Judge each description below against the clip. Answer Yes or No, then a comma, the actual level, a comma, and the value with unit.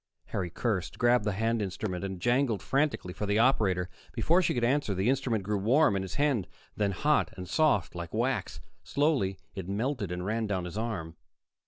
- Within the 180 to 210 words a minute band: Yes, average, 190 wpm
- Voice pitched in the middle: No, low, 105 Hz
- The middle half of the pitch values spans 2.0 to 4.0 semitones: No, average, 4.7 semitones